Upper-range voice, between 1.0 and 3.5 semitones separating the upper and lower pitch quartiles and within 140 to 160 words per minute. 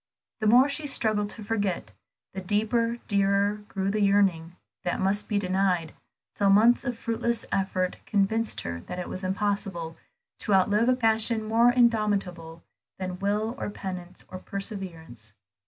Yes: high, 200 Hz; average, 3.0 semitones; average, 150 wpm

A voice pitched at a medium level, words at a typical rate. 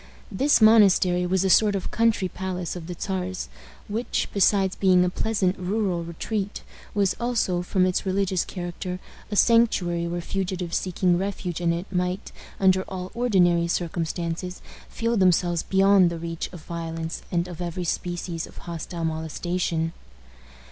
Yes: medium, 180 Hz; average, 150 wpm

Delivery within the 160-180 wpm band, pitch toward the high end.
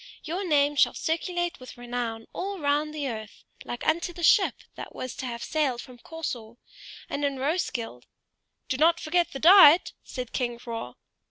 Yes: average, 175 wpm; very high, 285 Hz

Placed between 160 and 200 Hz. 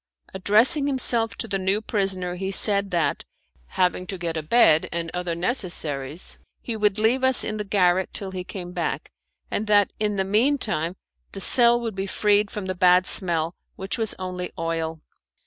Yes: high, 190 Hz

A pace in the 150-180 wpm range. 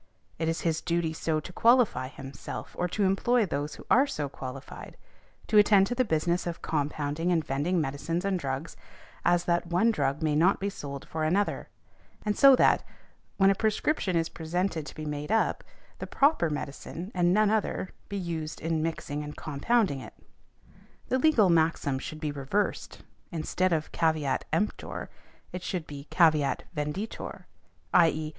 Yes: average, 165 wpm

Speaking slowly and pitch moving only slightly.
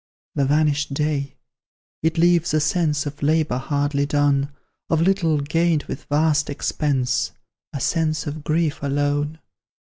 Yes: slow, 130 wpm; narrow, 1.8 semitones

